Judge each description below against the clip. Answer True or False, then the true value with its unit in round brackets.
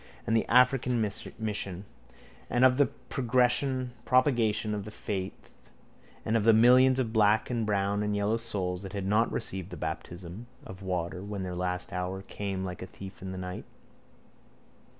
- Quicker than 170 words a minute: False (165 wpm)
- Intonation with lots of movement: False (3.9 semitones)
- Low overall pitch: True (105 Hz)